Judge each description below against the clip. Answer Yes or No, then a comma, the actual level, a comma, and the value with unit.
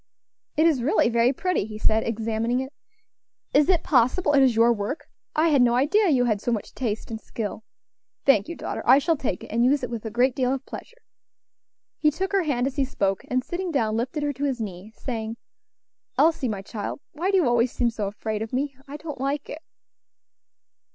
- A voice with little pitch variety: No, average, 4.5 semitones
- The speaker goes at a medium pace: No, fast, 215 wpm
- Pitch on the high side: Yes, very high, 255 Hz